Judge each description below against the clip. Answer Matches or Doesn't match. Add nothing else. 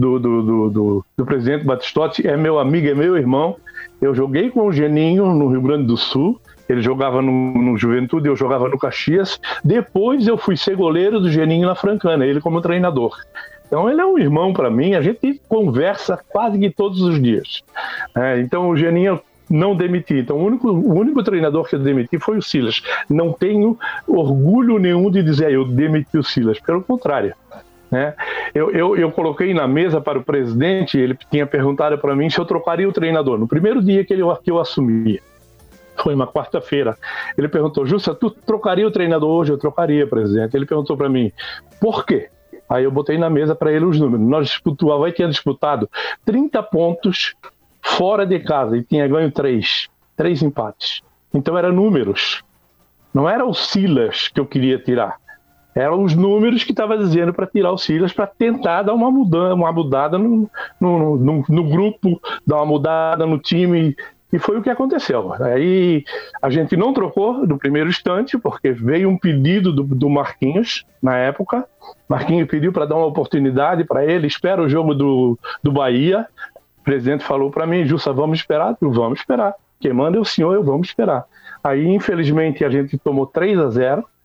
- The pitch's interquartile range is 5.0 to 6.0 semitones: Matches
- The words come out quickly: Matches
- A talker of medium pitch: Matches